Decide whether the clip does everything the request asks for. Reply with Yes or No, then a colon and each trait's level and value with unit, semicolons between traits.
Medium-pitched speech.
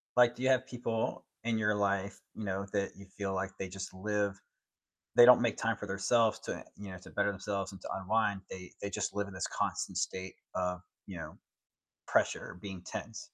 No: low, 100 Hz